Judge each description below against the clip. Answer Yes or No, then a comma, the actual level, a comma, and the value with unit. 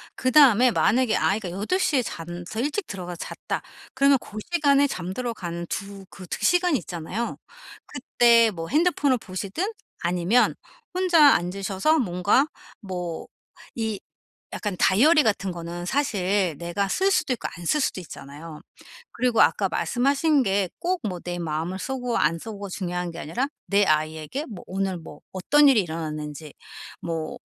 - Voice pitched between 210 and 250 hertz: No, high, 200 Hz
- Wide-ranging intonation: Yes, wide, 7.1 semitones